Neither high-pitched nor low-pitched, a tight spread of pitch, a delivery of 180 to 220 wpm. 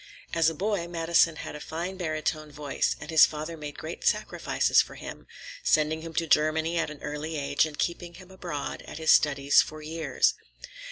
Yes: medium, 160 Hz; narrow, 1.9 semitones; average, 185 wpm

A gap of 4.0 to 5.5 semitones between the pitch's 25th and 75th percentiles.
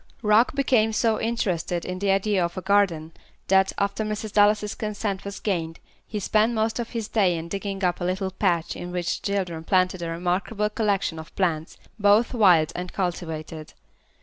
No: average, 3.2 semitones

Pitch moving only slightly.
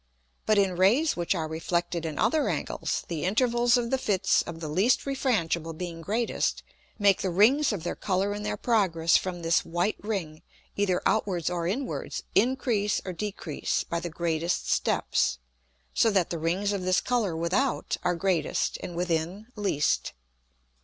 No: average, 4.1 semitones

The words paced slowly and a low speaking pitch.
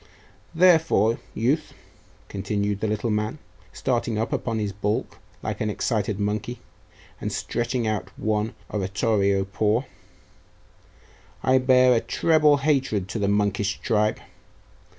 Yes: slow, 120 wpm; low, 110 Hz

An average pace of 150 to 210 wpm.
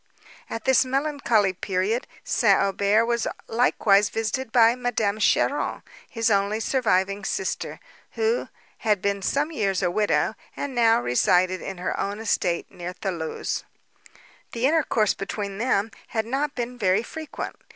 No: average, 140 wpm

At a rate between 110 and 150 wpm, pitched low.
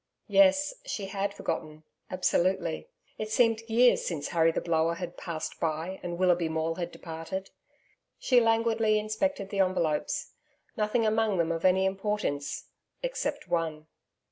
No: average, 140 wpm; high, 190 Hz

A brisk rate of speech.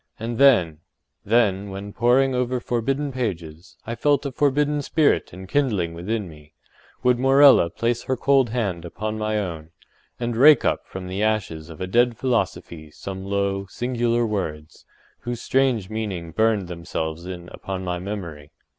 No: average, 145 wpm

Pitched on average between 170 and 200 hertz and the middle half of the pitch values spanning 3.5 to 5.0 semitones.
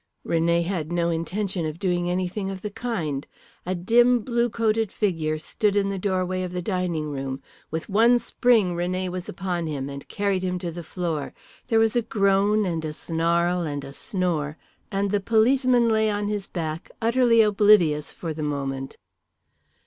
Yes: medium, 185 Hz; average, 4.3 semitones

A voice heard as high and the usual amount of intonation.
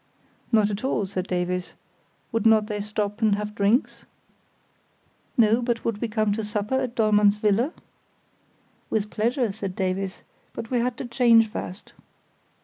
No: high, 215 Hz; narrow, 2.2 semitones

